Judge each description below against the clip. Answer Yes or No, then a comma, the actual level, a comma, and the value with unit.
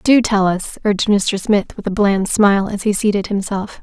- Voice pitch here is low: No, high, 205 Hz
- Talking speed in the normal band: No, fast, 220 wpm